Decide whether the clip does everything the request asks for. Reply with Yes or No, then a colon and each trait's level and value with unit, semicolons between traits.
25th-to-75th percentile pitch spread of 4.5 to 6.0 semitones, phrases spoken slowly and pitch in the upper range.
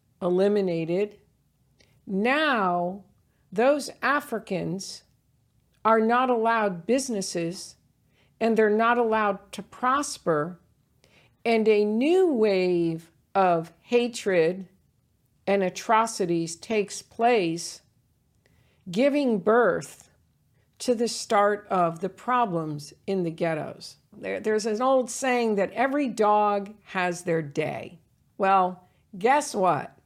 Yes: average, 5.0 semitones; slow, 100 wpm; high, 200 Hz